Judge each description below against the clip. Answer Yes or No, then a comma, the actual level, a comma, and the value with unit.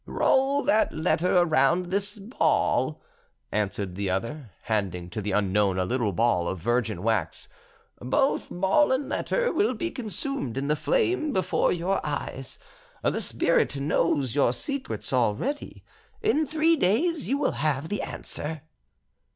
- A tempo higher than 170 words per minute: No, average, 145 wpm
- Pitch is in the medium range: Yes, medium, 155 Hz